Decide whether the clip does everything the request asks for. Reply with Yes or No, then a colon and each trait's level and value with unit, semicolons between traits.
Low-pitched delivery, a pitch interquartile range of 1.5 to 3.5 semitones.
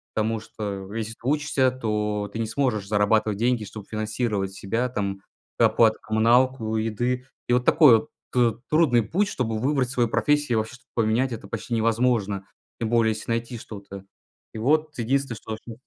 Yes: low, 115 Hz; average, 2.7 semitones